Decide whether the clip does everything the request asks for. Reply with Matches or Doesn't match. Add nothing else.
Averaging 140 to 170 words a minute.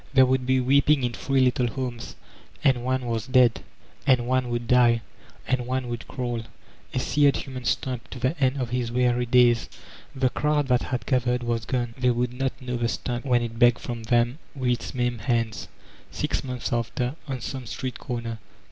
Doesn't match